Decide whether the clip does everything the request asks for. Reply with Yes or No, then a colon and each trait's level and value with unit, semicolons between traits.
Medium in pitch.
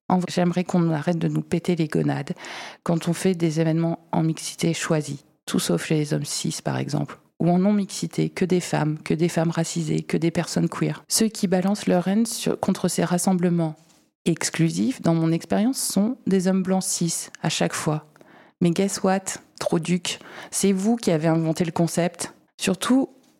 Yes: medium, 175 Hz